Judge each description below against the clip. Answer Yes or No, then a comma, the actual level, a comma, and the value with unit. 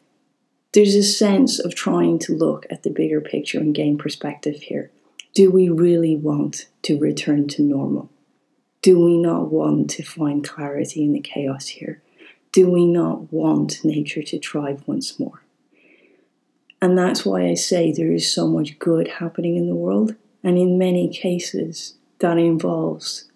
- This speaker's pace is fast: No, average, 160 wpm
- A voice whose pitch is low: No, medium, 170 Hz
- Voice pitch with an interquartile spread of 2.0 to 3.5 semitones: No, average, 4.5 semitones